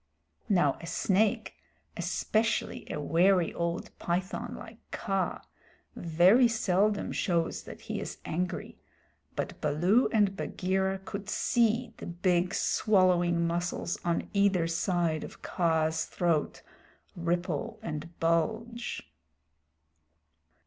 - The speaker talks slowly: Yes, slow, 105 wpm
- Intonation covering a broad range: No, average, 3.1 semitones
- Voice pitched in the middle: Yes, medium, 180 Hz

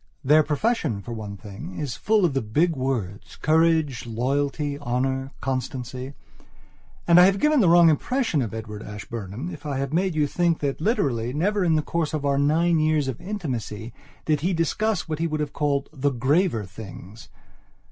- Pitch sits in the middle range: Yes, medium, 145 Hz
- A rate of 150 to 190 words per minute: Yes, average, 180 wpm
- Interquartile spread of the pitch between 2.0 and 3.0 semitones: No, average, 5.1 semitones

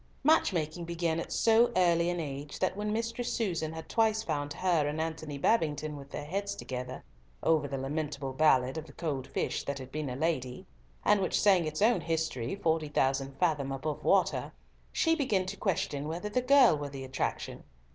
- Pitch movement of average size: Yes, average, 4.9 semitones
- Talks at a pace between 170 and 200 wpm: Yes, average, 190 wpm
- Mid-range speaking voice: Yes, medium, 160 Hz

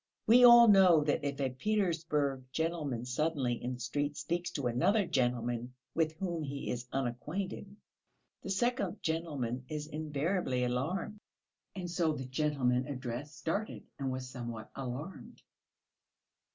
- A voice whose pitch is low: No, medium, 145 Hz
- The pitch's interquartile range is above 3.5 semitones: Yes, average, 5.2 semitones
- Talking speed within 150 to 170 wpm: No, slow, 135 wpm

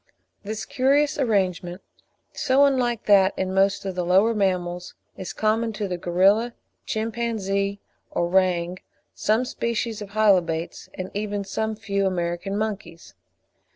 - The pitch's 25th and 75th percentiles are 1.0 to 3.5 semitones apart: Yes, average, 3.1 semitones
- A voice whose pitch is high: Yes, high, 200 Hz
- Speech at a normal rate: No, slow, 130 wpm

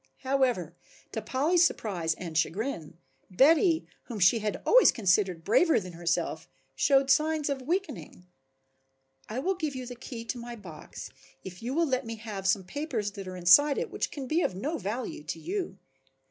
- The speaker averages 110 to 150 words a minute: No, average, 175 wpm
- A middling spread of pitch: No, wide, 7.3 semitones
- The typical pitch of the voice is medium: No, high, 235 Hz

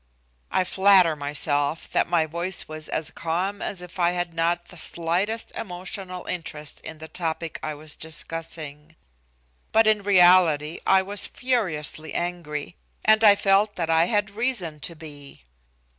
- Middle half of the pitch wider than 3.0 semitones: Yes, average, 3.5 semitones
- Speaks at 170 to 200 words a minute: No, average, 150 wpm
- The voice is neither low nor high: Yes, medium, 170 Hz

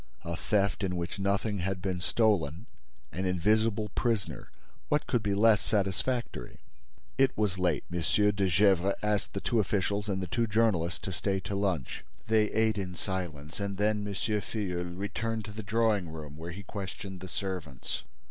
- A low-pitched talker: Yes, low, 100 Hz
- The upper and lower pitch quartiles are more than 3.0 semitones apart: No, average, 2.7 semitones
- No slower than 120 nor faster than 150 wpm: No, average, 165 wpm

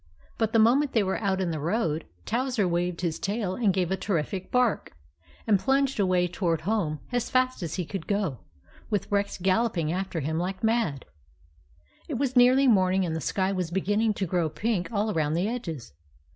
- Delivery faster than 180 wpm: Yes, average, 195 wpm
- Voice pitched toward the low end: No, high, 190 Hz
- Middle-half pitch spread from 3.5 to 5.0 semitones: Yes, average, 4.5 semitones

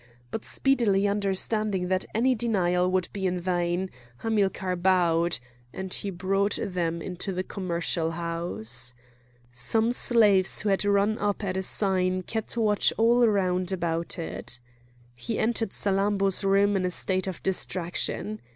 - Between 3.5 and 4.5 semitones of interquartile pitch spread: No, narrow, 2.4 semitones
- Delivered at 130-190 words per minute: Yes, average, 140 wpm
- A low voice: No, high, 190 Hz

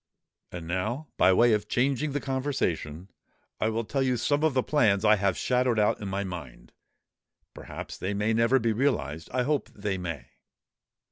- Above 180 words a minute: No, average, 175 wpm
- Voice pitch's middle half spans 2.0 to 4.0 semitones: No, wide, 5.5 semitones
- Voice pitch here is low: Yes, low, 110 Hz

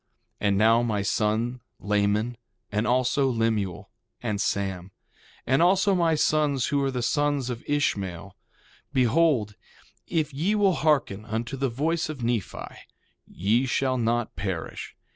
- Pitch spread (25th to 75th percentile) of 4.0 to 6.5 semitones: Yes, wide, 5.4 semitones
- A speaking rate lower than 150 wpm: Yes, average, 140 wpm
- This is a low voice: Yes, low, 120 Hz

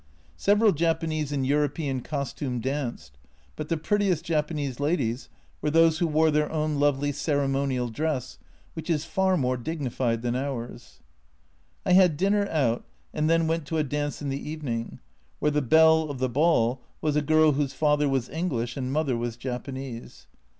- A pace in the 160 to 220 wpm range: Yes, average, 170 wpm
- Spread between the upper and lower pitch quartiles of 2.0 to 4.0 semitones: Yes, average, 3.4 semitones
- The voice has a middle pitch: Yes, medium, 145 Hz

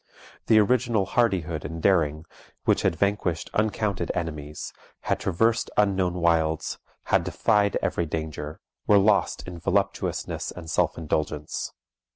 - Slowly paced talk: Yes, slow, 125 wpm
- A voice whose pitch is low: Yes, very low, 85 Hz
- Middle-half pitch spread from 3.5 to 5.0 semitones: Yes, average, 4.4 semitones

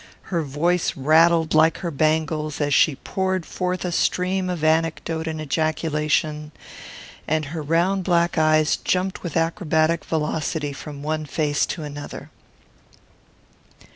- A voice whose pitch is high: No, medium, 160 Hz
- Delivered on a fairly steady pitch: Yes, narrow, 2.0 semitones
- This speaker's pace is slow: Yes, slow, 130 wpm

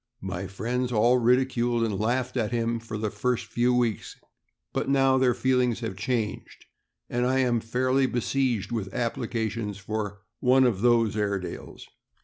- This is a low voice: Yes, low, 120 Hz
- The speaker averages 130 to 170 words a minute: Yes, average, 150 wpm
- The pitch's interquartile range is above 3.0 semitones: No, average, 2.7 semitones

